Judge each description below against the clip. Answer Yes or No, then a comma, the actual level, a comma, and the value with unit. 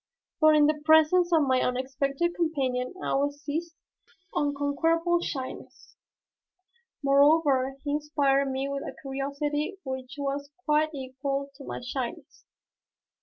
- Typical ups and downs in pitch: No, narrow, 2.2 semitones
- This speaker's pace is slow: Yes, slow, 130 wpm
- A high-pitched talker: Yes, very high, 285 Hz